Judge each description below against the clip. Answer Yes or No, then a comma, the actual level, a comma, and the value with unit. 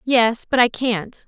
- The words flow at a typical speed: Yes, average, 190 wpm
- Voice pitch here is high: Yes, high, 235 Hz